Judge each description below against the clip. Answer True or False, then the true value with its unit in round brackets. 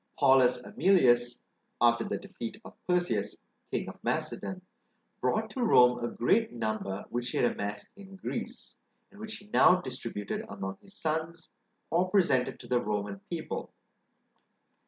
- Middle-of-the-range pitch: False (125 Hz)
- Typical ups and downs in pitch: False (7.7 semitones)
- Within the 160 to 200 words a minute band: False (145 wpm)